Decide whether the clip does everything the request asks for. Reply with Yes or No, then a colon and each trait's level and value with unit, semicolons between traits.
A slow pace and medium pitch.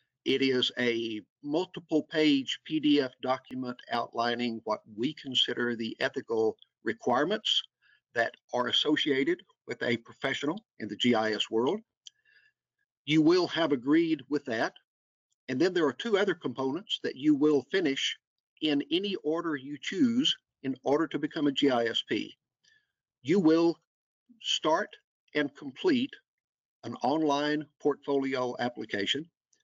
Yes: slow, 125 wpm; medium, 150 Hz